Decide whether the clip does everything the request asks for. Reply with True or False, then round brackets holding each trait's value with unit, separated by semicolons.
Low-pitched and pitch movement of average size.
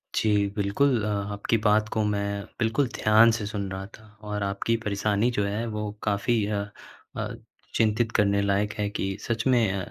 False (105 Hz; 1.8 semitones)